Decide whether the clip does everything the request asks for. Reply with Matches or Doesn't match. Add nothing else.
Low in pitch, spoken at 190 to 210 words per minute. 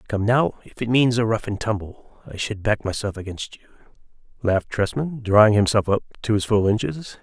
Matches